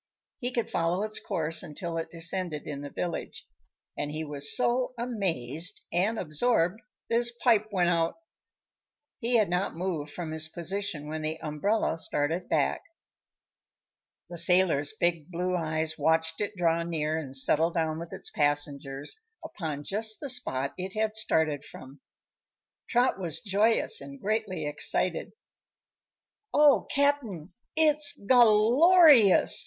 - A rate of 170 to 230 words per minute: No, average, 140 wpm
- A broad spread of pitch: Yes, wide, 5.7 semitones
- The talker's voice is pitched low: No, medium, 175 Hz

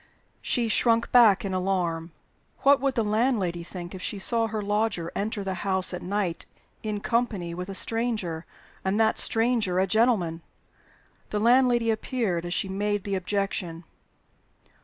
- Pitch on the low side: No, high, 205 Hz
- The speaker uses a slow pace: No, average, 155 wpm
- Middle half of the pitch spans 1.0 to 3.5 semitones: No, average, 3.9 semitones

